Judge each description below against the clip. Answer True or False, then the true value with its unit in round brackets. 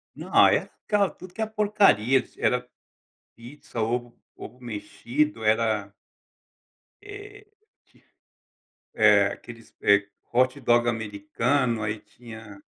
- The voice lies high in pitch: False (120 Hz)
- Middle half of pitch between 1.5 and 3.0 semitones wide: False (4.8 semitones)